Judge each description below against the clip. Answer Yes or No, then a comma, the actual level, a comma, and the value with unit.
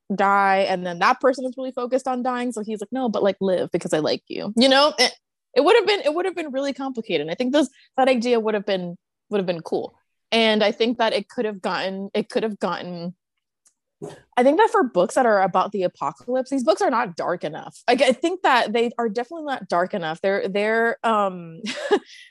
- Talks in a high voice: Yes, high, 230 Hz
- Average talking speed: No, fast, 235 wpm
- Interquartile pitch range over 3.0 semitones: Yes, average, 5.0 semitones